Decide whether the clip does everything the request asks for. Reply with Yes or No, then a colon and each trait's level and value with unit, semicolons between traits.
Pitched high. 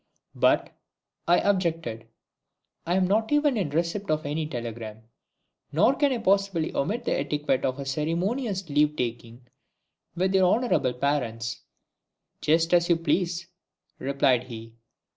No: medium, 160 Hz